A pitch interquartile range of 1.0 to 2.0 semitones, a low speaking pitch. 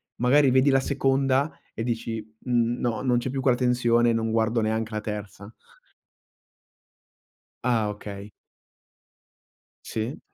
No: narrow, 2.6 semitones; low, 120 Hz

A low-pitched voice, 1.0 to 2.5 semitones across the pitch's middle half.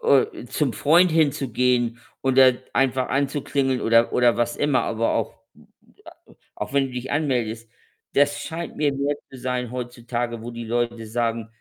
No: low, 125 Hz; average, 2.9 semitones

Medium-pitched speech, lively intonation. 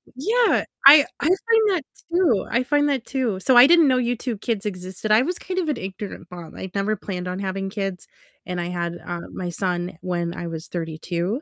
No: high, 200 Hz; wide, 6.7 semitones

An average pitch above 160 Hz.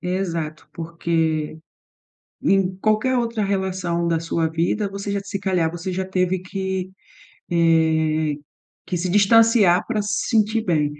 Yes: medium, 185 Hz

